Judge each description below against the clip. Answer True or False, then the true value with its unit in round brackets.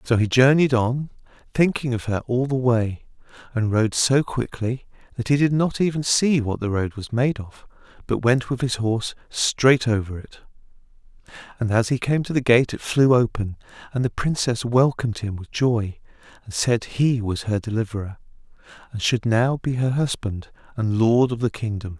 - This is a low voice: True (120 Hz)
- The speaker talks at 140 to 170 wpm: False (185 wpm)